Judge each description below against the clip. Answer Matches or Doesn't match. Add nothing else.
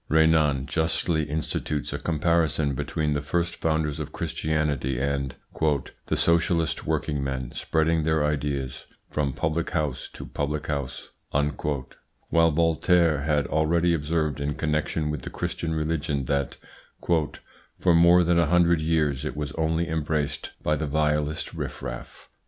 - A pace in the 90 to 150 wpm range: Matches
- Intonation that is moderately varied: Doesn't match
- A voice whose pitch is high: Doesn't match